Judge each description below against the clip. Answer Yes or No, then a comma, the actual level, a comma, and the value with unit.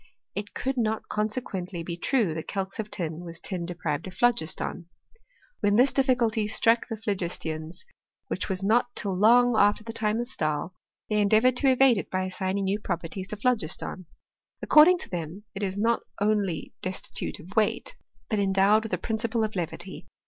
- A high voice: Yes, high, 205 Hz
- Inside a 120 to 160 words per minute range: No, average, 180 wpm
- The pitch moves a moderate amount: Yes, average, 3.7 semitones